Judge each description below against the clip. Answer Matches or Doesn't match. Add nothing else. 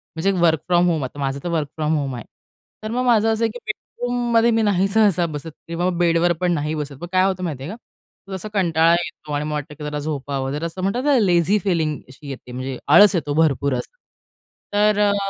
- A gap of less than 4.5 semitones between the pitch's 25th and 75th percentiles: Doesn't match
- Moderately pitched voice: Matches